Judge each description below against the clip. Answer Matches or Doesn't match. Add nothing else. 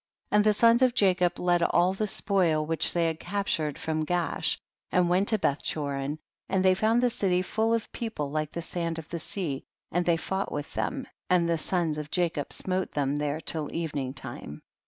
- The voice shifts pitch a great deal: Doesn't match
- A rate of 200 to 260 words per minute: Matches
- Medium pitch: Matches